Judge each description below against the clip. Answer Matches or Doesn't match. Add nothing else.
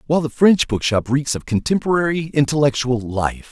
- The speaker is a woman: Doesn't match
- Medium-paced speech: Matches